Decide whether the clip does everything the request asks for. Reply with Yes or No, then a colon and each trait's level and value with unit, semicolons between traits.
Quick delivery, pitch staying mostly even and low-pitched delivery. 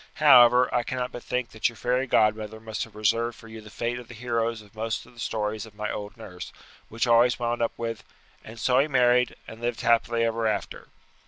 Yes: fast, 225 wpm; narrow, 1.8 semitones; low, 115 Hz